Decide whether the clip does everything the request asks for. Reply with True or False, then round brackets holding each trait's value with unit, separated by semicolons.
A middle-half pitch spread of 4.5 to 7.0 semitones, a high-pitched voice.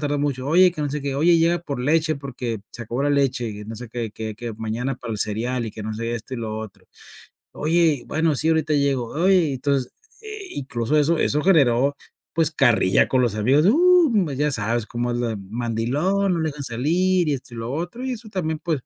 False (5.5 semitones; 140 Hz)